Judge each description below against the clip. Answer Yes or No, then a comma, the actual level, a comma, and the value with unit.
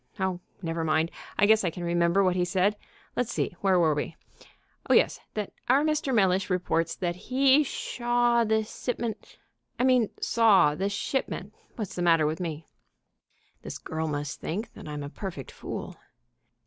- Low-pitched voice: No, medium, 185 Hz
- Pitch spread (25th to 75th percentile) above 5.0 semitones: Yes, wide, 5.6 semitones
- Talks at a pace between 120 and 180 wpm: Yes, average, 170 wpm